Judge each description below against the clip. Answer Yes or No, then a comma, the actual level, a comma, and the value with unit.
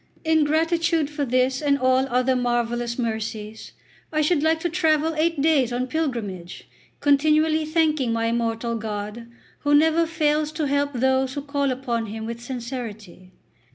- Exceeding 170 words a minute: No, average, 155 wpm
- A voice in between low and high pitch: No, very high, 265 Hz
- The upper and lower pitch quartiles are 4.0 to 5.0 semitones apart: Yes, average, 4.7 semitones